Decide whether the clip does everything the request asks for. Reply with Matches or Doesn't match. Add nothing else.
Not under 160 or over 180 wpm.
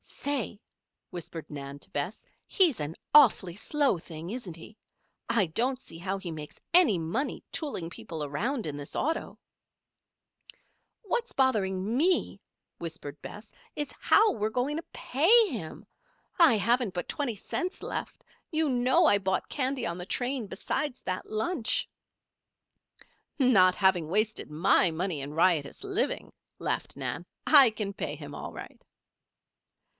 Doesn't match